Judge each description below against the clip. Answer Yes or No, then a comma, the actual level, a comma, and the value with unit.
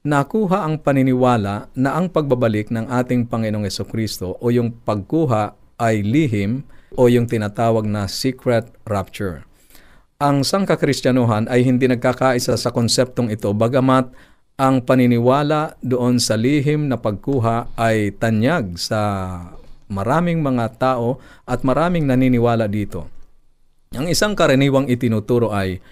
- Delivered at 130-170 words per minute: No, average, 120 wpm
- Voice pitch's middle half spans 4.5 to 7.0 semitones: No, average, 3.2 semitones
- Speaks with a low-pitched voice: Yes, low, 125 Hz